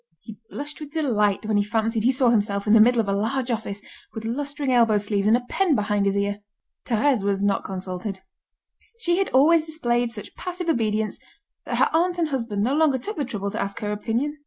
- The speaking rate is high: Yes, fast, 215 wpm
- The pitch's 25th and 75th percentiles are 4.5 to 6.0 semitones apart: Yes, wide, 5.6 semitones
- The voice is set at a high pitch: Yes, high, 230 Hz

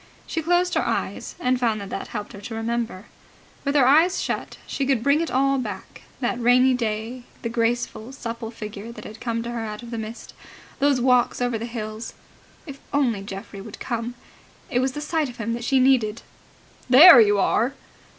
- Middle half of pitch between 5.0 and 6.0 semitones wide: No, average, 3.0 semitones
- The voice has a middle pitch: No, high, 240 Hz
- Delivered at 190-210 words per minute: Yes, average, 200 wpm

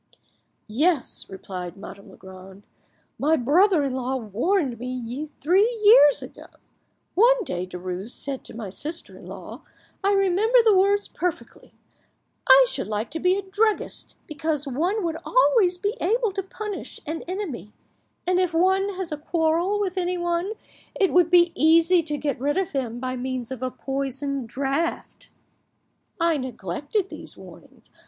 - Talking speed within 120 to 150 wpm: Yes, average, 145 wpm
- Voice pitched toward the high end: Yes, very high, 320 Hz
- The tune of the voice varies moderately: No, wide, 6.8 semitones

